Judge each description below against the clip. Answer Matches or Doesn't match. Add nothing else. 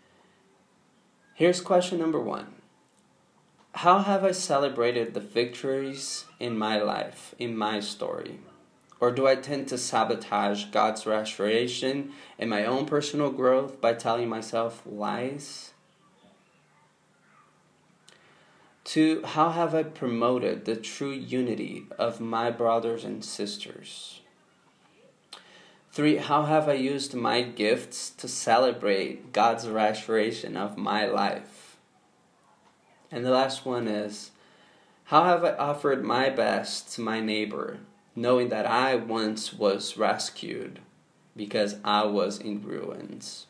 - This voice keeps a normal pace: Doesn't match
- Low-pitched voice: Matches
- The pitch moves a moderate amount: Matches